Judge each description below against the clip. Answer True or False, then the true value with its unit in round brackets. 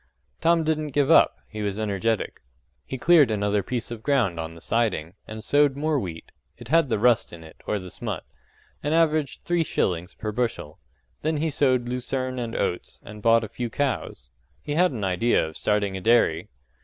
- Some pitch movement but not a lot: False (6.0 semitones)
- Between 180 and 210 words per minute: True (190 wpm)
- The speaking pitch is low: True (115 Hz)